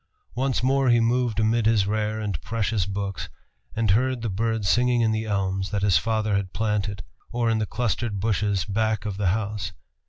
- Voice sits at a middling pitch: No, low, 110 Hz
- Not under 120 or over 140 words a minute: No, average, 190 wpm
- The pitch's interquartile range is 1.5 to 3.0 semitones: Yes, narrow, 2.4 semitones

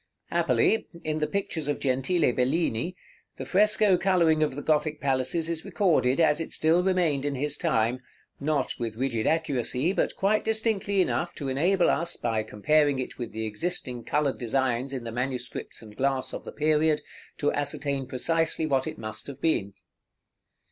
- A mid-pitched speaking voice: Yes, medium, 145 Hz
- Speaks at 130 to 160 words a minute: No, average, 170 wpm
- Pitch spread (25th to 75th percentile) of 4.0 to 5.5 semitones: Yes, average, 4.5 semitones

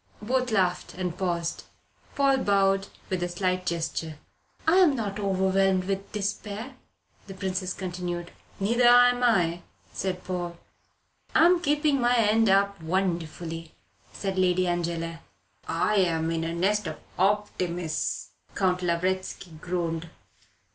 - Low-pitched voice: No, medium, 185 Hz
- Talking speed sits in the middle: No, slow, 125 wpm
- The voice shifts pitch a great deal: No, average, 3.2 semitones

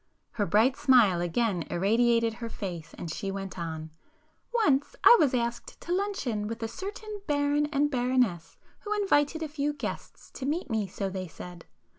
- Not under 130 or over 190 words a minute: Yes, average, 165 wpm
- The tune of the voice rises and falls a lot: Yes, wide, 7.2 semitones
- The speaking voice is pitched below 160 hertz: No, high, 240 Hz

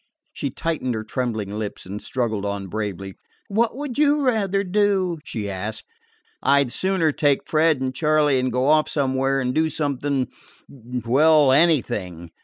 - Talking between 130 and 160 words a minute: Yes, average, 155 wpm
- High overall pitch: No, low, 135 Hz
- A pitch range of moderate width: No, wide, 6.4 semitones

